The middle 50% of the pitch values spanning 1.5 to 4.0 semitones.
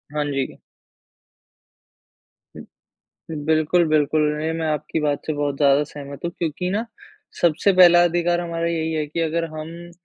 Yes: narrow, 2.5 semitones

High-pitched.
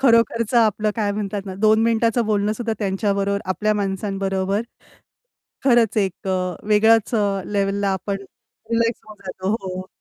Yes: high, 205 Hz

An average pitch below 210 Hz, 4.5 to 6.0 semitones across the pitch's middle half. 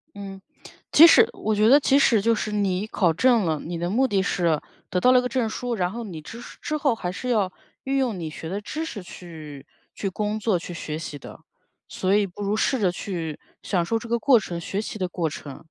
Yes: high, 200 Hz; average, 4.9 semitones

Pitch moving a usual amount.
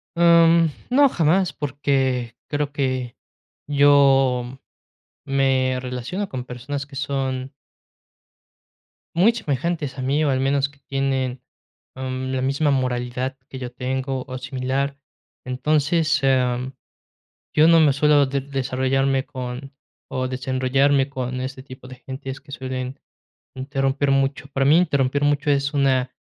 No: narrow, 1.7 semitones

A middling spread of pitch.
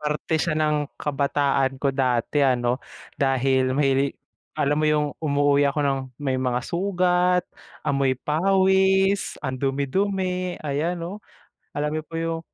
Yes: average, 4.3 semitones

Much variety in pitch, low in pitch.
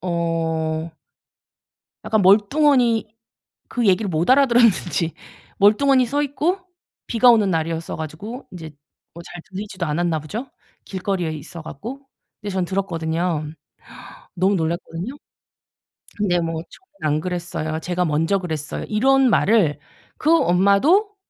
No: wide, 5.7 semitones; medium, 185 Hz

